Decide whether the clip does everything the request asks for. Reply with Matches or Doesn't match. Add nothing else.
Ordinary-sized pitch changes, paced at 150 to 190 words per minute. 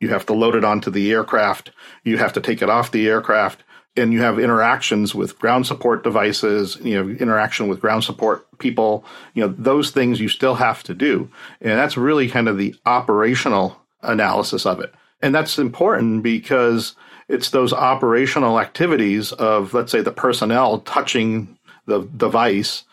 Doesn't match